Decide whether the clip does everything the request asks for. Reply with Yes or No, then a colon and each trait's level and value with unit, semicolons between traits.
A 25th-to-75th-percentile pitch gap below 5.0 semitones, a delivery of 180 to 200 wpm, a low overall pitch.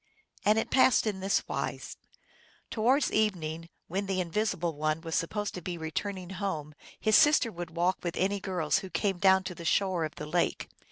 No: average, 3.5 semitones; average, 185 wpm; medium, 185 Hz